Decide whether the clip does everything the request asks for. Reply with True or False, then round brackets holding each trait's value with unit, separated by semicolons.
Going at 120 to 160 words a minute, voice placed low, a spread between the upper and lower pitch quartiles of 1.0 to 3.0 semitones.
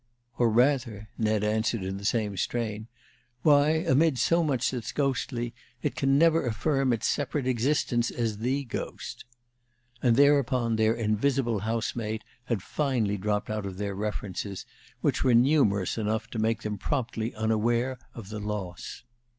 False (150 wpm; 115 Hz; 3.7 semitones)